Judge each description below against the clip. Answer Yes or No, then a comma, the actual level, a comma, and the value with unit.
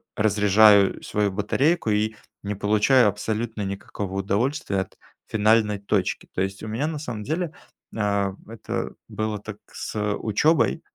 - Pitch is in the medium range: No, low, 105 Hz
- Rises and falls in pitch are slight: Yes, narrow, 2.1 semitones